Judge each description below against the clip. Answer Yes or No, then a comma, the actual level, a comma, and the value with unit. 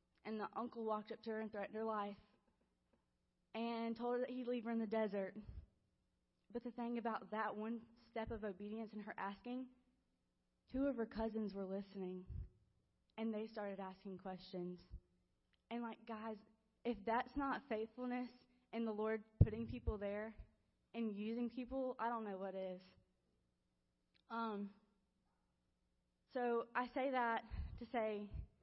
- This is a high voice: Yes, high, 220 Hz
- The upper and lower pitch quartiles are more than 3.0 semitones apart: No, average, 2.7 semitones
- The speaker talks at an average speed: Yes, average, 150 wpm